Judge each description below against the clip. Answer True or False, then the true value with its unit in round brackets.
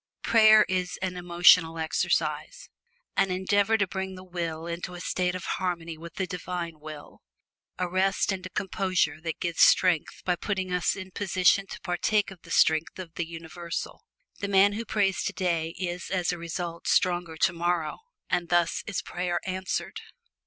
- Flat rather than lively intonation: True (2.0 semitones)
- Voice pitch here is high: False (180 Hz)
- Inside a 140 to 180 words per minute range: True (165 wpm)